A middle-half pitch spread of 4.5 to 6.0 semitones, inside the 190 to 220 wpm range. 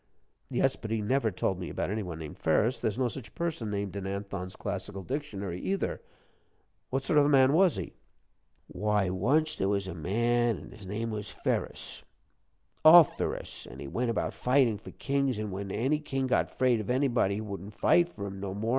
Yes: average, 5.1 semitones; average, 200 wpm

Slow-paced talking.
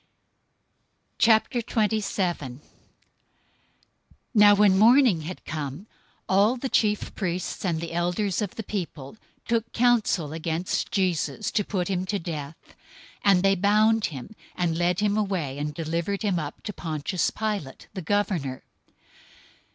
Yes: slow, 130 wpm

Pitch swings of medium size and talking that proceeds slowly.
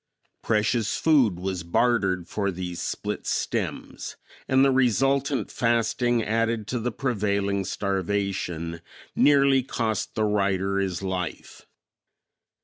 Yes: average, 4.0 semitones; slow, 105 wpm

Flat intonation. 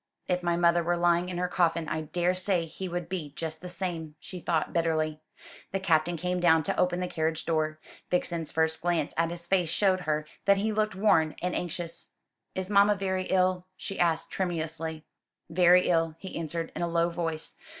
Yes: narrow, 1.9 semitones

